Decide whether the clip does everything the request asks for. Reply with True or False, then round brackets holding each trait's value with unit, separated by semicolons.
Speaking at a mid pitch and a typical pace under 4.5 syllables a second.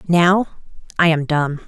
True (165 Hz; 4.0 syllables/s)